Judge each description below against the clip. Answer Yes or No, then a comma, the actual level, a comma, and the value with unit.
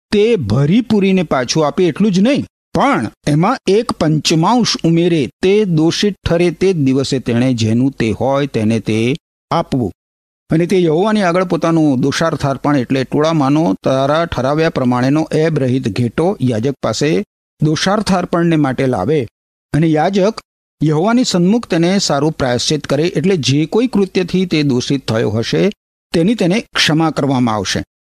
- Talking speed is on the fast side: Yes, fast, 145 wpm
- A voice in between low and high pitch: Yes, medium, 155 Hz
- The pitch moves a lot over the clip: Yes, wide, 5.7 semitones